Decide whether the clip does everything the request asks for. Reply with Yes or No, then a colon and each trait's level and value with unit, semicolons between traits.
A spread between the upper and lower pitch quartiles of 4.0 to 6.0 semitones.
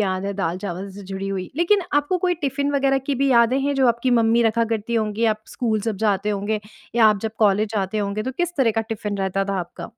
Yes: average, 4.6 semitones